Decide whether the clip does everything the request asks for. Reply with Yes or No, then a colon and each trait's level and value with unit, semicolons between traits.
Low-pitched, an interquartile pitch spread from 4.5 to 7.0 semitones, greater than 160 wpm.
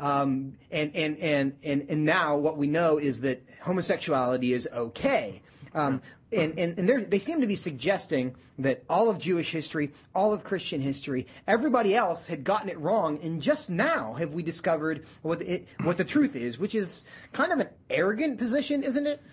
No: medium, 160 Hz; wide, 5.4 semitones; average, 185 wpm